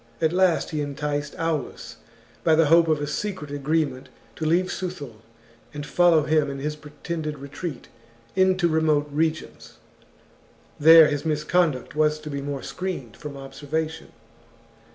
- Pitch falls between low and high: Yes, medium, 155 Hz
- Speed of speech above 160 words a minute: No, average, 145 wpm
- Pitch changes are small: Yes, narrow, 2.2 semitones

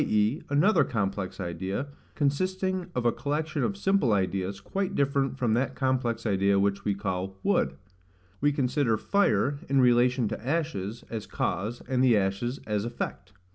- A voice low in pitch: Yes, low, 120 Hz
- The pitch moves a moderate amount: No, wide, 6.1 semitones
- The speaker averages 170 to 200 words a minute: No, average, 155 wpm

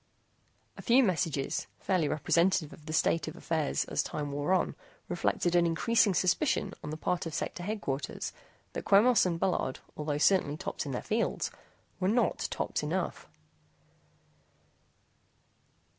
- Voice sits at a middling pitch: Yes, medium, 170 Hz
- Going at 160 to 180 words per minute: No, average, 145 wpm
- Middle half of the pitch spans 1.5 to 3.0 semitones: No, average, 4.3 semitones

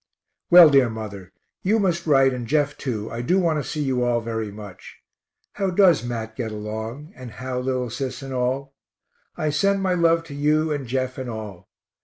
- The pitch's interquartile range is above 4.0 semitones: Yes, average, 5.0 semitones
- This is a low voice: Yes, low, 130 Hz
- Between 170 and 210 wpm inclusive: Yes, average, 195 wpm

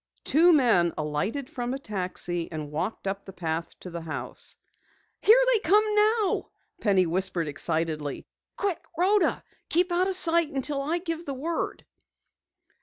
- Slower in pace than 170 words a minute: Yes, average, 150 wpm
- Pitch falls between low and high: No, very high, 250 Hz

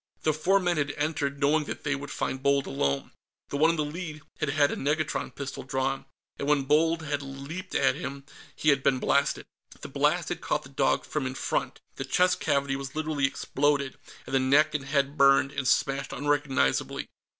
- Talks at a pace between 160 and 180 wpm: No, average, 200 wpm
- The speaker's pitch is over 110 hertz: Yes, medium, 140 Hz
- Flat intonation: Yes, narrow, 1.9 semitones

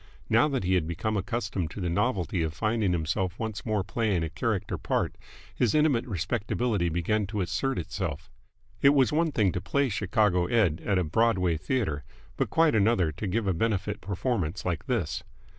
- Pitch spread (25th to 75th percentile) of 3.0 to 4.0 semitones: No, average, 4.5 semitones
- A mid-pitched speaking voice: No, low, 100 Hz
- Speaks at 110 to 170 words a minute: No, average, 180 wpm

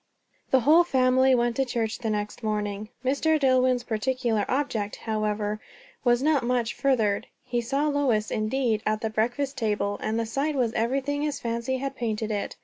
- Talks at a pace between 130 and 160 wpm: No, average, 170 wpm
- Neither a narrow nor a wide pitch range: Yes, average, 3.7 semitones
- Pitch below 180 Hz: No, high, 240 Hz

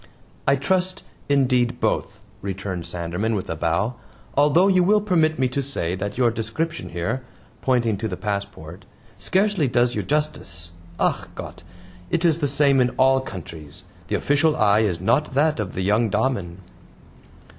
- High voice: No, low, 120 Hz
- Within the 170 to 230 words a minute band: No, average, 160 wpm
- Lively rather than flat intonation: Yes, wide, 7.0 semitones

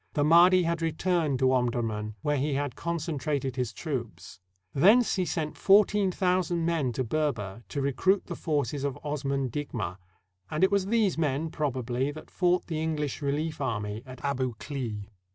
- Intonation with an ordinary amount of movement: Yes, average, 4.6 semitones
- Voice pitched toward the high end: No, medium, 145 Hz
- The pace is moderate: Yes, average, 170 wpm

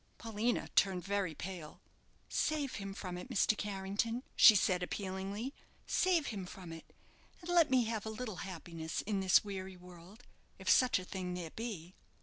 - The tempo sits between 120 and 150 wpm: No, average, 165 wpm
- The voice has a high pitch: Yes, high, 195 Hz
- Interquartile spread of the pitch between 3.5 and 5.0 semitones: Yes, average, 3.8 semitones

